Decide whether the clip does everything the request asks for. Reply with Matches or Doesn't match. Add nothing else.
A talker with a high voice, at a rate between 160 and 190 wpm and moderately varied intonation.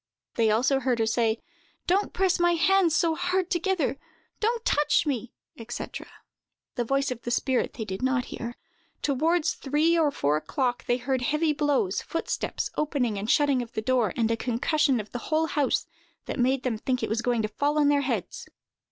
Matches